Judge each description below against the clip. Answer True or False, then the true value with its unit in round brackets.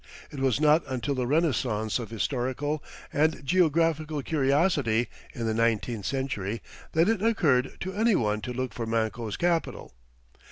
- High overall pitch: False (135 Hz)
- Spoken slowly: False (150 wpm)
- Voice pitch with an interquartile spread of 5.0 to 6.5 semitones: True (5.4 semitones)